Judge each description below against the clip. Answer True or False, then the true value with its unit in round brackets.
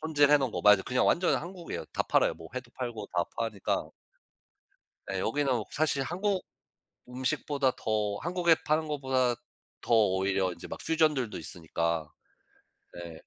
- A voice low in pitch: True (125 Hz)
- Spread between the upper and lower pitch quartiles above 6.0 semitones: True (7.0 semitones)